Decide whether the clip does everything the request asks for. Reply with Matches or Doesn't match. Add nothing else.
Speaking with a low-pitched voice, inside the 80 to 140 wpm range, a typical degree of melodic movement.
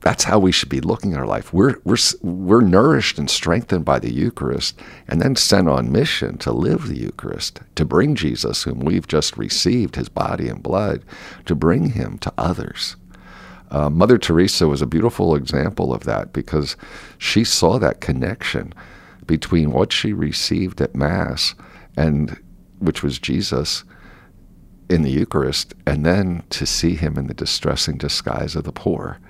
Doesn't match